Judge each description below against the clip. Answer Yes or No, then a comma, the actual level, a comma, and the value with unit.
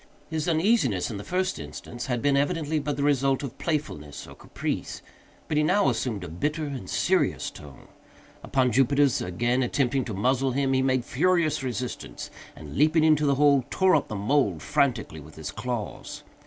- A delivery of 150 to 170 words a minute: No, average, 180 wpm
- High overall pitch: No, low, 135 Hz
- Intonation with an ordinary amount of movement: Yes, average, 4.2 semitones